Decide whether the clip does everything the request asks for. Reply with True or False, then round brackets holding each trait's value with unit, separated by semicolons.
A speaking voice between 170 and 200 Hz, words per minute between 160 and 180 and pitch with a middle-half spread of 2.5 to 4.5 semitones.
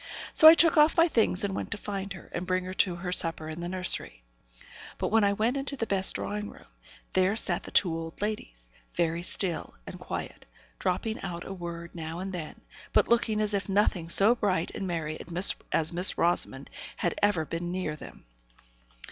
False (185 Hz; 200 wpm; 3.4 semitones)